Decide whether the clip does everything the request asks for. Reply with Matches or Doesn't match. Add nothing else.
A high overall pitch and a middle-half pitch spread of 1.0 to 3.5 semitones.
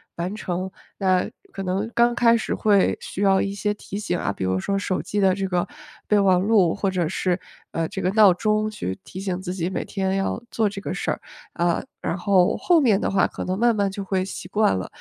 Matches